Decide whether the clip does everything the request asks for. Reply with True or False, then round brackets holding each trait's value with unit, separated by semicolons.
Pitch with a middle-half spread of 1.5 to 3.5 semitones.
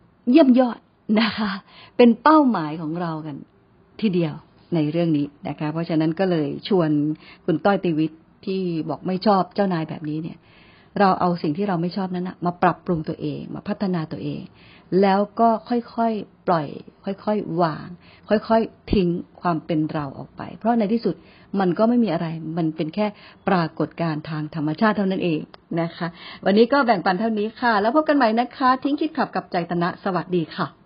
False (4.5 semitones)